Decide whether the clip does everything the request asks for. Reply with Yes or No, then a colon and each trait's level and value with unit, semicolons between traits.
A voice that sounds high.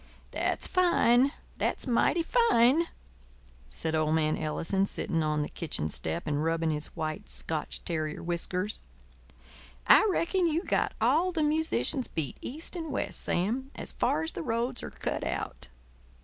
Yes: high, 195 Hz